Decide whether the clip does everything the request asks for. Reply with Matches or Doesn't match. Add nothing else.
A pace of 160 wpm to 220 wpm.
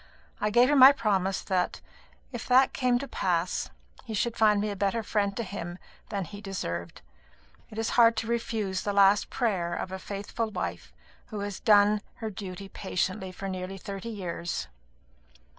Matches